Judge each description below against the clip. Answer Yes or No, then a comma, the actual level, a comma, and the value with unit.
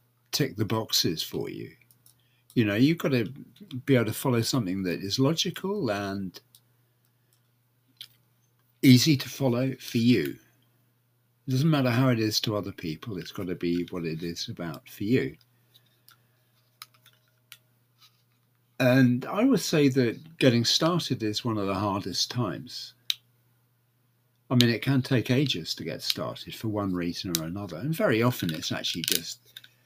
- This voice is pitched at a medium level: No, low, 120 Hz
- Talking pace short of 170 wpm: Yes, average, 155 wpm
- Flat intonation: Yes, narrow, 2.2 semitones